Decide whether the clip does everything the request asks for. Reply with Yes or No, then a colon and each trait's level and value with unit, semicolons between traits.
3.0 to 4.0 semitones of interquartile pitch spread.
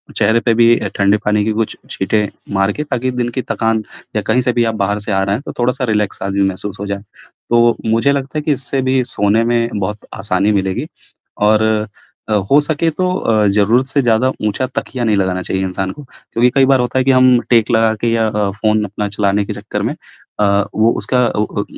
Yes: average, 3.4 semitones